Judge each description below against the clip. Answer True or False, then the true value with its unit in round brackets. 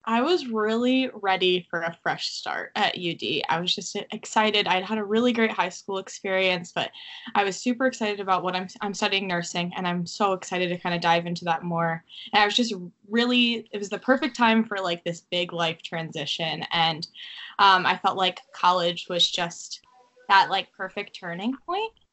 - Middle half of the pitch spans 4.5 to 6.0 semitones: False (4.0 semitones)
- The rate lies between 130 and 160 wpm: False (200 wpm)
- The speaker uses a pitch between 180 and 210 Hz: True (190 Hz)